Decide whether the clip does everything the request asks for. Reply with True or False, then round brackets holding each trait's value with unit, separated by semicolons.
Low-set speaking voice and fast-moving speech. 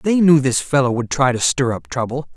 True (130 Hz; 255 wpm)